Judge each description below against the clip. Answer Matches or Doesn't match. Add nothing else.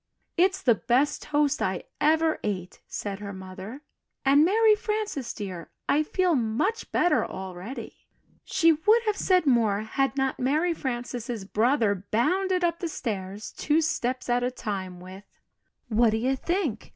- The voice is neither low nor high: Doesn't match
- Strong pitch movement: Matches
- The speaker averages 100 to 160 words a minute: Matches